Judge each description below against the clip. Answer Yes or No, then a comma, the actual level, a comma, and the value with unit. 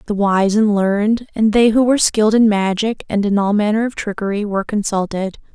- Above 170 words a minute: Yes, fast, 205 wpm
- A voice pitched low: No, high, 210 Hz